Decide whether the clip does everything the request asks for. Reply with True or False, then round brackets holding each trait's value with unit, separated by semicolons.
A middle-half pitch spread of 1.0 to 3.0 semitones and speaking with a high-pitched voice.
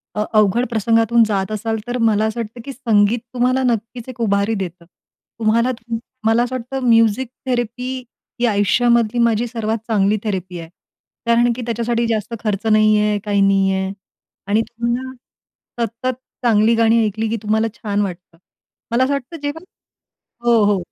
True (2.4 semitones; 225 Hz)